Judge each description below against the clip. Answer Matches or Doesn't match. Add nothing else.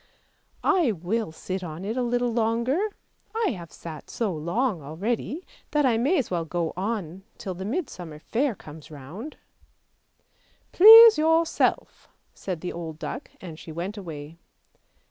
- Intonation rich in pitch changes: Matches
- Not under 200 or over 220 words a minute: Doesn't match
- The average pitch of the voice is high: Matches